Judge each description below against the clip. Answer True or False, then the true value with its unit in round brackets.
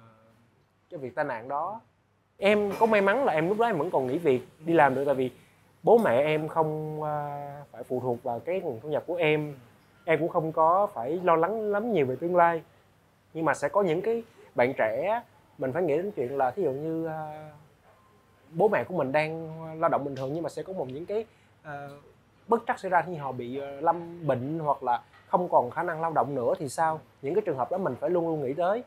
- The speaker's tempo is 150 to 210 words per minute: False (235 wpm)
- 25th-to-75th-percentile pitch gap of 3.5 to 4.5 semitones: True (4.0 semitones)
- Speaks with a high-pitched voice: False (155 Hz)